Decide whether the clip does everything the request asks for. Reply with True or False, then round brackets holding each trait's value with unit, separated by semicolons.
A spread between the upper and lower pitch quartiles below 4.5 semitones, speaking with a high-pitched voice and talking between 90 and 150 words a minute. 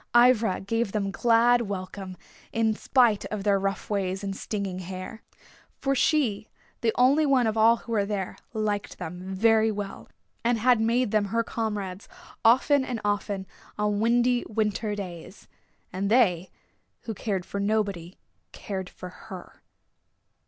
True (2.9 semitones; 210 Hz; 145 wpm)